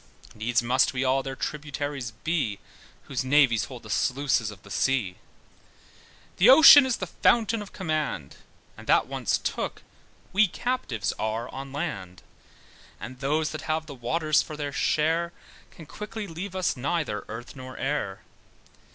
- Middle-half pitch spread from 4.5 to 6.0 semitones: Yes, average, 5.2 semitones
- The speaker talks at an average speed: Yes, average, 150 wpm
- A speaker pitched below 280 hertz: Yes, medium, 140 Hz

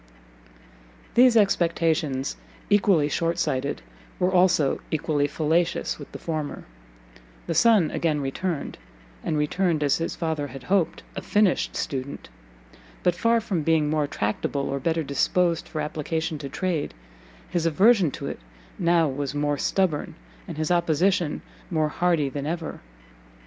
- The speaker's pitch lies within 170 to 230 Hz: No, medium, 160 Hz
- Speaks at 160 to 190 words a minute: No, slow, 135 wpm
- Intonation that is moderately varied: Yes, average, 3.4 semitones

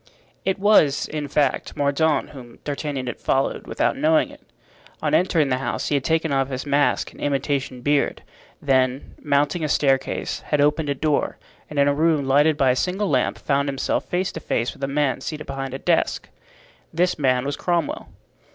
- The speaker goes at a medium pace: Yes, average, 190 wpm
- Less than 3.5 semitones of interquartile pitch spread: Yes, narrow, 2.5 semitones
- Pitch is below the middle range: No, medium, 145 Hz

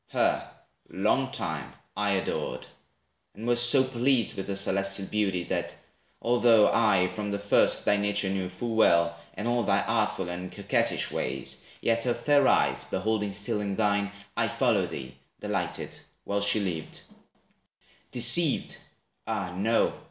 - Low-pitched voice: Yes, low, 105 Hz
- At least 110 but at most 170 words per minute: Yes, average, 145 wpm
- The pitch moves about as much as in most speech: Yes, average, 3.1 semitones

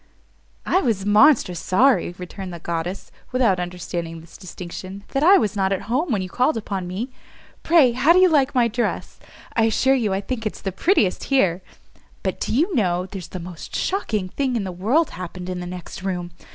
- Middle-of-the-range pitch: No, high, 200 Hz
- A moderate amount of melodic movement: No, wide, 5.9 semitones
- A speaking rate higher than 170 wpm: Yes, average, 200 wpm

